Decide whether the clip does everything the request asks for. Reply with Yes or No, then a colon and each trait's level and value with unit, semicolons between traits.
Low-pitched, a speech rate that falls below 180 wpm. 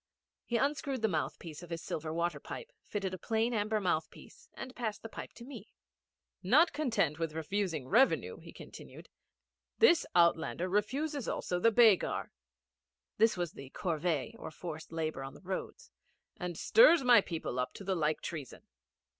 No: high, 190 Hz; average, 165 wpm